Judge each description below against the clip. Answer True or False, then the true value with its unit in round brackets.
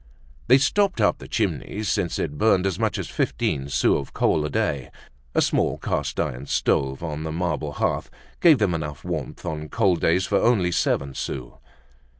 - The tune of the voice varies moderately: False (6.2 semitones)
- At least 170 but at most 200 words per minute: True (180 wpm)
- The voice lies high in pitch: False (80 Hz)